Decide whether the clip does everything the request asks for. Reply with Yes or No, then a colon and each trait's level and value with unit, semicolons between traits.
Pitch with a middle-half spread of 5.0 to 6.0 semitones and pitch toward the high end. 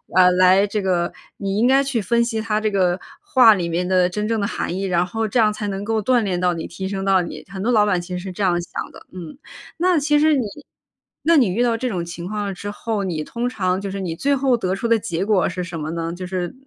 No: average, 3.8 semitones; high, 195 Hz